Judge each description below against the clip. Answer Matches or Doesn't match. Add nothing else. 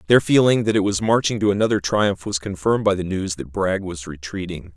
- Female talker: Doesn't match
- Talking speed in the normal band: Doesn't match